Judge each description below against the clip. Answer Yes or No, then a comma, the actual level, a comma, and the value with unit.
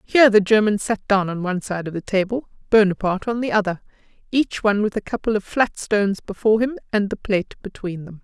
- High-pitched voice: Yes, high, 205 Hz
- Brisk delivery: Yes, fast, 220 wpm